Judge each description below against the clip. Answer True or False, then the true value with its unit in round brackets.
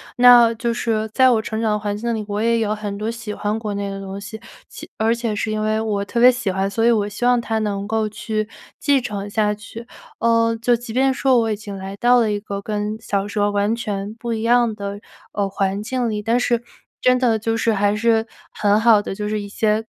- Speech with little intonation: True (2.1 semitones)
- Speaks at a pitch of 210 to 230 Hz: True (220 Hz)